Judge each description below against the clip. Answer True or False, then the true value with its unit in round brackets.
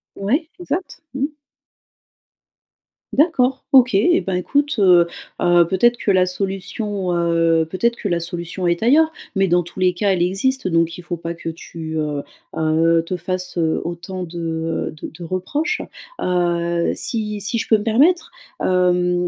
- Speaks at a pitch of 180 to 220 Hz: True (185 Hz)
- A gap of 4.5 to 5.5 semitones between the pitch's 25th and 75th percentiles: True (4.8 semitones)